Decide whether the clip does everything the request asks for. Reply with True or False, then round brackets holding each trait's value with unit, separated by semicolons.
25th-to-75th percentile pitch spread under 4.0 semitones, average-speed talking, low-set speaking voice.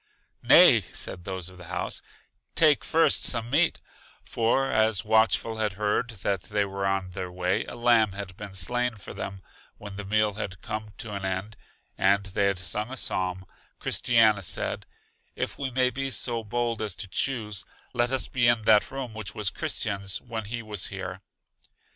True (3.4 semitones; 180 wpm; 105 Hz)